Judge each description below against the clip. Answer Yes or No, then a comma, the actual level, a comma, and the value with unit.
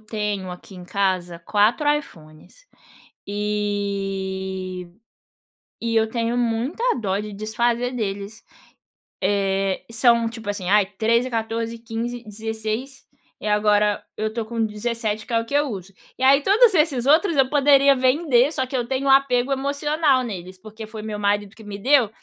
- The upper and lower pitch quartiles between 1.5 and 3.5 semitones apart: No, average, 3.9 semitones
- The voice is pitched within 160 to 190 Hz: No, high, 225 Hz